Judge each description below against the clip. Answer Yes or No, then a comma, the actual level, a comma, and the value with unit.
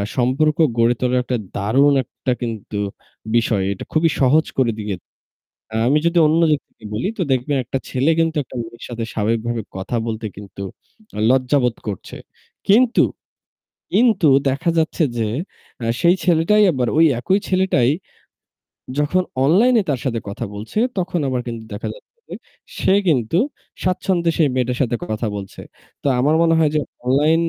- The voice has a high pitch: No, low, 130 Hz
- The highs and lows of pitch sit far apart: Yes, wide, 5.8 semitones